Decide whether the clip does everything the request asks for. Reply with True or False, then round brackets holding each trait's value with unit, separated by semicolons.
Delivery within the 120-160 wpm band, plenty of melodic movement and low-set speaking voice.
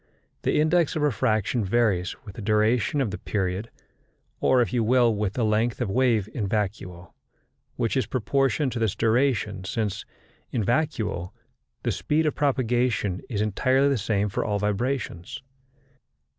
False (155 wpm; 3.9 semitones; 115 Hz)